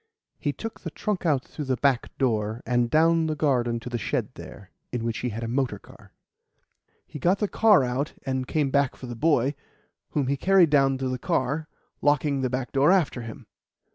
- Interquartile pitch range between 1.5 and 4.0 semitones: Yes, average, 3.6 semitones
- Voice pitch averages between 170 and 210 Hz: No, low, 135 Hz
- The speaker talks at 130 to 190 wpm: No, fast, 205 wpm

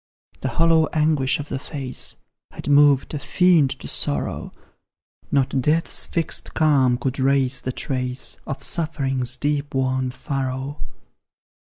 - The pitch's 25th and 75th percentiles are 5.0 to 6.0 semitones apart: No, narrow, 2.4 semitones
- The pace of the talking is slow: Yes, slow, 130 wpm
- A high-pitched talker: No, low, 135 Hz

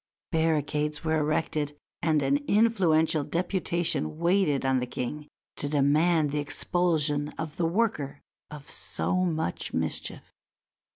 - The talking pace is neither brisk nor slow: No, slow, 120 wpm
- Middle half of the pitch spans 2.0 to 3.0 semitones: Yes, average, 2.7 semitones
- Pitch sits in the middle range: Yes, medium, 155 Hz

